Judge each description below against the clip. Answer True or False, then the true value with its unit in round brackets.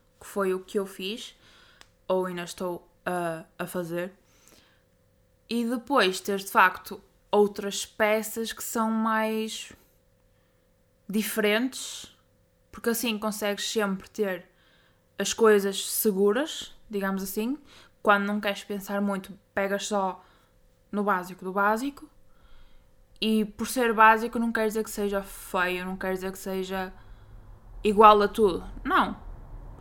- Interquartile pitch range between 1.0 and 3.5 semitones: True (2.6 semitones)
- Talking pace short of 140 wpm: True (125 wpm)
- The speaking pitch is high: True (205 Hz)